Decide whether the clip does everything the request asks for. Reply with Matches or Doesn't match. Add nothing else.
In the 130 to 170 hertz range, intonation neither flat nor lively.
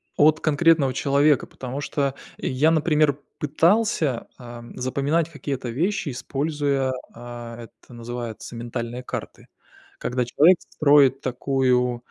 Matches